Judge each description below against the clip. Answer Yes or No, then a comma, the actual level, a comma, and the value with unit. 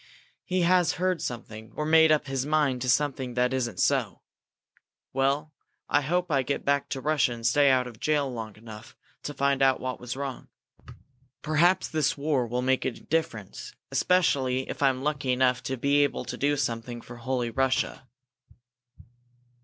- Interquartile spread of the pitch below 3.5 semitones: Yes, average, 3.0 semitones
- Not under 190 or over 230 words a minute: No, average, 170 wpm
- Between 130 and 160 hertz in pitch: Yes, low, 135 Hz